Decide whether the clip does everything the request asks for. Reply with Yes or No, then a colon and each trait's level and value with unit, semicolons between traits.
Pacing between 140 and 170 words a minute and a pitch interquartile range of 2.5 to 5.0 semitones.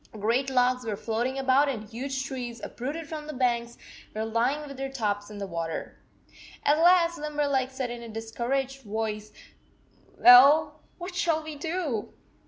Yes: average, 160 wpm; average, 4.4 semitones